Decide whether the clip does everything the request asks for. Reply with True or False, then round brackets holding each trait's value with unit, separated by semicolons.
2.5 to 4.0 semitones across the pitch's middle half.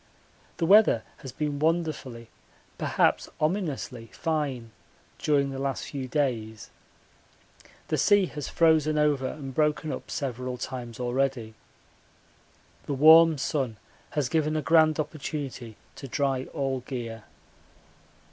True (3.5 semitones)